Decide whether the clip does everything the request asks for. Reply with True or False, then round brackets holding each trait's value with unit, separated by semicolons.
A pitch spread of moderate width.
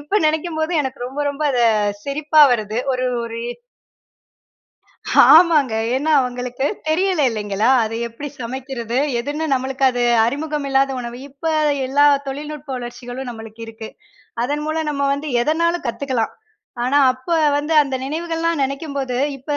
True (3.7 semitones)